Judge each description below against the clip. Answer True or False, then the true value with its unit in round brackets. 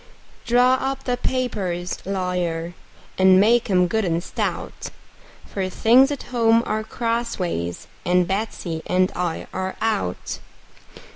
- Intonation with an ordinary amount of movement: True (4.7 semitones)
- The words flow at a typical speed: False (125 wpm)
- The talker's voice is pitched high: True (195 Hz)